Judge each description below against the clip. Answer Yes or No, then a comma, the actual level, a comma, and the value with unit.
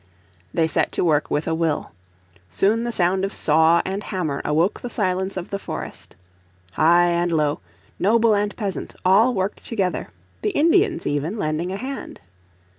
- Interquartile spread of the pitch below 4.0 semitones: No, average, 4.4 semitones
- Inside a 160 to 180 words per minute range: Yes, average, 165 wpm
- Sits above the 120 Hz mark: Yes, medium, 185 Hz